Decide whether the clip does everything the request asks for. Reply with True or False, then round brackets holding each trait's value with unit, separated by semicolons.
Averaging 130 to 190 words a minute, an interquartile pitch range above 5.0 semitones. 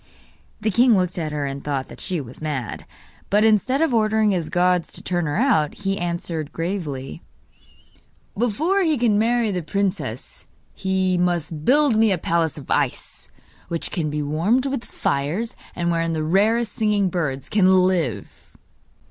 True (165 wpm; 5.5 semitones)